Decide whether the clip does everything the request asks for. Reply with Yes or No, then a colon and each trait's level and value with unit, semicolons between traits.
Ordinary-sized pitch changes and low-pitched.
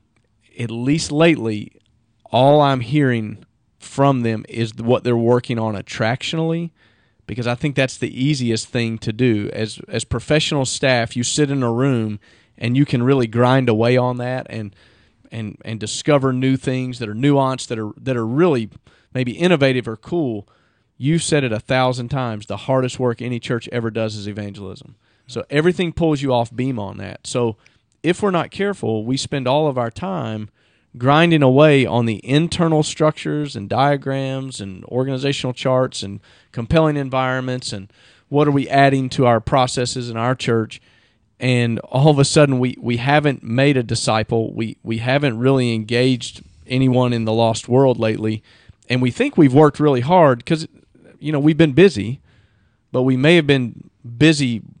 Yes: average, 3.7 semitones; low, 125 Hz